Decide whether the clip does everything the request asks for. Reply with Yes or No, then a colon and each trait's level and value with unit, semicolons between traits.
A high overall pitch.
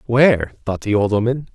No: low, 115 Hz